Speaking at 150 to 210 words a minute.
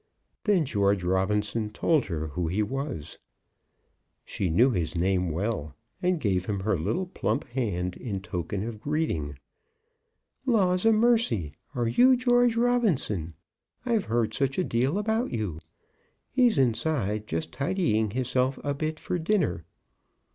No: average, 140 wpm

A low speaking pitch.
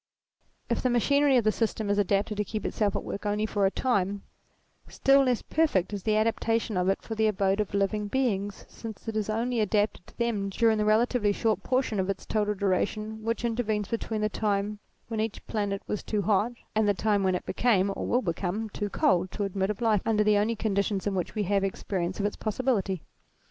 No: high, 210 Hz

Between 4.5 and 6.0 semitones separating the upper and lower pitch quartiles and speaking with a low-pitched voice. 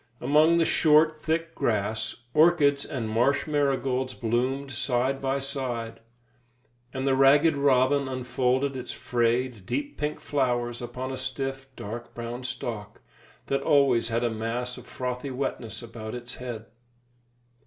No: average, 2.7 semitones; low, 130 Hz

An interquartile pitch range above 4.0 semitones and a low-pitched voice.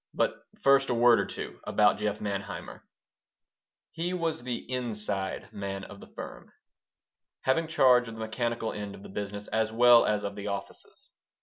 No: average, 3.5 semitones; low, 110 Hz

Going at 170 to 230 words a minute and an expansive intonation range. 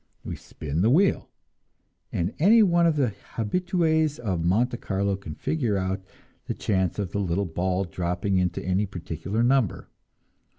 No: average, 155 wpm; wide, 7.0 semitones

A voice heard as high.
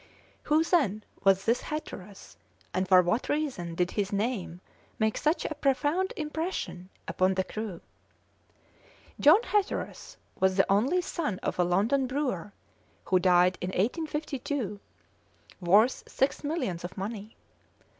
Yes: high, 215 Hz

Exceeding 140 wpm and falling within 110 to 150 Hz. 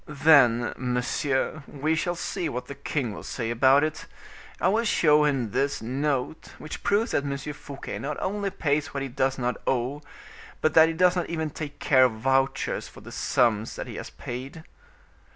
Yes: average, 190 wpm; medium, 140 Hz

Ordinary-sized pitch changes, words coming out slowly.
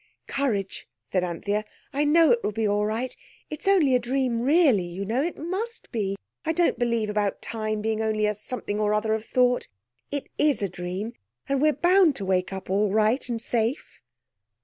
No: average, 4.9 semitones; average, 195 wpm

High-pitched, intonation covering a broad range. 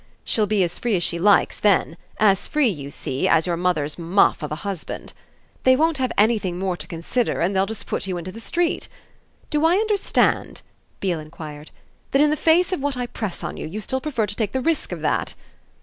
Yes: high, 205 Hz; wide, 7.1 semitones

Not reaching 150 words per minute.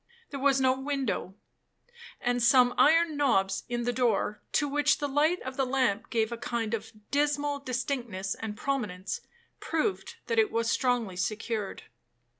No: average, 155 wpm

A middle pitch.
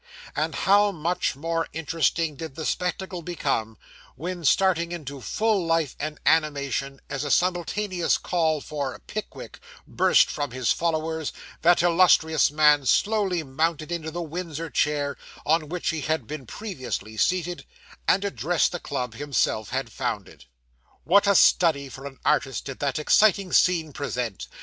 Yes: medium, 160 Hz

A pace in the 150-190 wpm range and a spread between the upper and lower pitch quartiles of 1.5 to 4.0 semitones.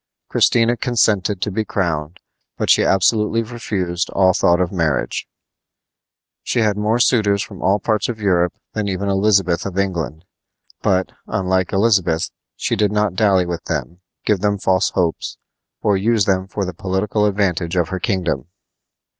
Yes: average, 155 wpm; average, 2.7 semitones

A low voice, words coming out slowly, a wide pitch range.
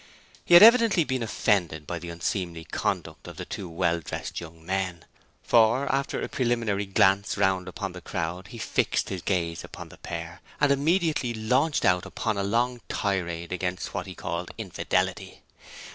No: very low, 95 Hz; average, 170 wpm; wide, 5.7 semitones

